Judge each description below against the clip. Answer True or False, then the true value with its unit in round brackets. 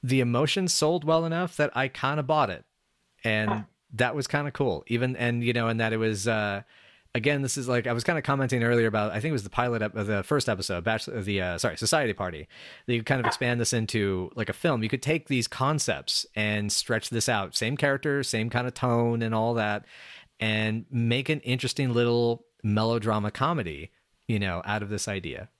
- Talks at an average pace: False (225 wpm)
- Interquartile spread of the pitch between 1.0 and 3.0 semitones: False (3.6 semitones)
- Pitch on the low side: True (120 Hz)